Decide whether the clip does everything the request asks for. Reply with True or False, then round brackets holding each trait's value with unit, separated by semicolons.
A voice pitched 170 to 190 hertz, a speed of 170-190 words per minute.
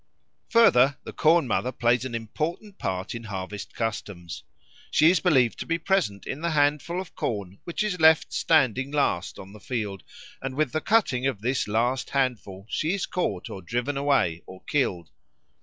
False (130 Hz; 175 wpm)